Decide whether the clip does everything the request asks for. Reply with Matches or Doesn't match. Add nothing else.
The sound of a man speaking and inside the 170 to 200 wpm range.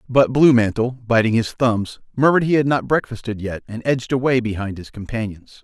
Matches